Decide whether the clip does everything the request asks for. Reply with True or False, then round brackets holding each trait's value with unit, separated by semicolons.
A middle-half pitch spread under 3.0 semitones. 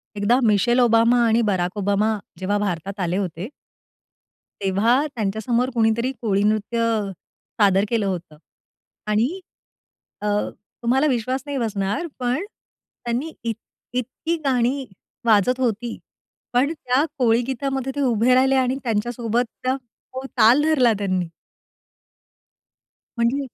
False (3.7 semitones)